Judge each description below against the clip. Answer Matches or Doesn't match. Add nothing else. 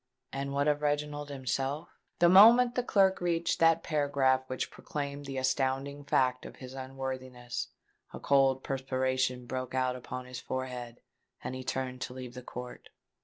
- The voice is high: Doesn't match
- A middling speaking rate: Matches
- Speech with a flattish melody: Matches